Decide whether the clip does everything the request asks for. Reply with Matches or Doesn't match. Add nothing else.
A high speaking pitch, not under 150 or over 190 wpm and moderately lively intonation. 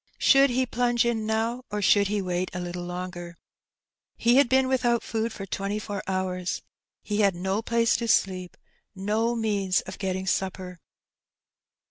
Matches